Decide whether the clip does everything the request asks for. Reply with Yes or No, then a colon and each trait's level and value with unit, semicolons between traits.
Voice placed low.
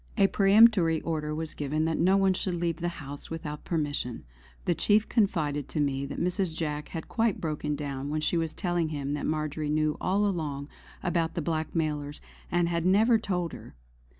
No: medium, 160 Hz